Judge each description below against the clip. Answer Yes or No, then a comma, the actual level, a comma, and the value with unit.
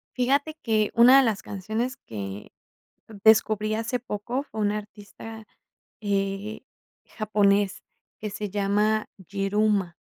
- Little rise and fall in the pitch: Yes, narrow, 1.9 semitones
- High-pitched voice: Yes, high, 210 Hz